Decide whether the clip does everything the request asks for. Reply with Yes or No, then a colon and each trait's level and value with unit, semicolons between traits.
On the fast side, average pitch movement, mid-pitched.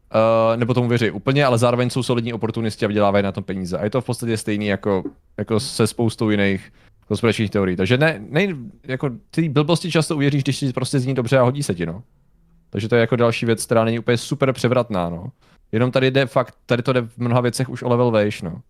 No: fast, 235 wpm; average, 3.6 semitones; low, 120 Hz